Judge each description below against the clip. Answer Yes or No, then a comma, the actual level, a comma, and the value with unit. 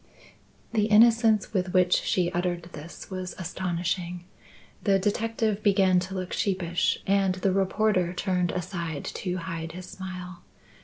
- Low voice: No, medium, 185 Hz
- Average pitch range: No, narrow, 1.9 semitones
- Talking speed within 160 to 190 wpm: No, slow, 135 wpm